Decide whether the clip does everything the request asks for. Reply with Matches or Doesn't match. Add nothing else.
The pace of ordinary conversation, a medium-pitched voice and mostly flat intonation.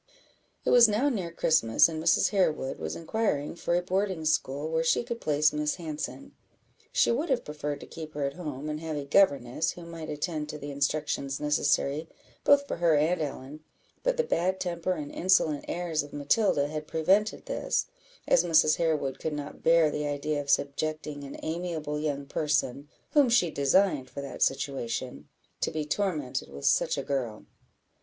Doesn't match